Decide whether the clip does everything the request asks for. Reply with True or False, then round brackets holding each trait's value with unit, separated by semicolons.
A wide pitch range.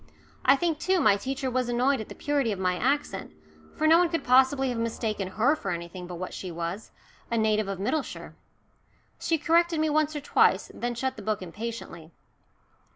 True (6.8 semitones)